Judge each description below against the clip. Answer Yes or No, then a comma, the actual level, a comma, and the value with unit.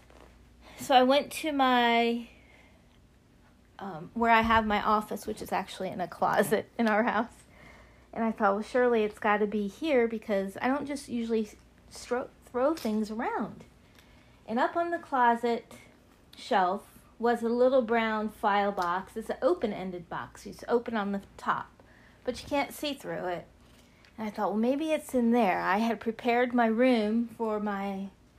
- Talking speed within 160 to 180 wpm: Yes, average, 175 wpm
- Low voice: No, high, 225 Hz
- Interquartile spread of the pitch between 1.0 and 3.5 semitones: Yes, average, 2.8 semitones